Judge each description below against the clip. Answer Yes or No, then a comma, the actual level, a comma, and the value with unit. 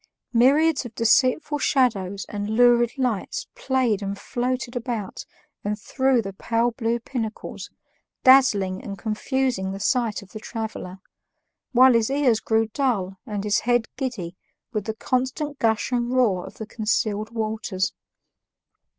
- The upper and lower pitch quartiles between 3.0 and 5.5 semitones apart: Yes, average, 3.5 semitones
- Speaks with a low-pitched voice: No, high, 230 Hz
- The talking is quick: No, average, 140 wpm